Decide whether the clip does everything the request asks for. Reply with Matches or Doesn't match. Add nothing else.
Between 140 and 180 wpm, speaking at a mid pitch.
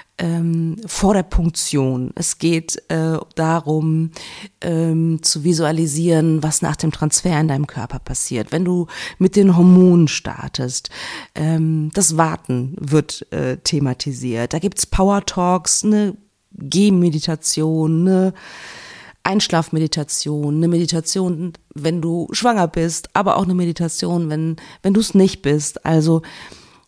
Doesn't match